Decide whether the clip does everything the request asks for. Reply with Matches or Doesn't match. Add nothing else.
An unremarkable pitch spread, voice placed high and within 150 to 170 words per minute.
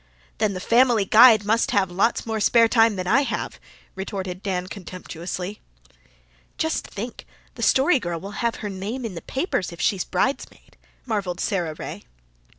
Matches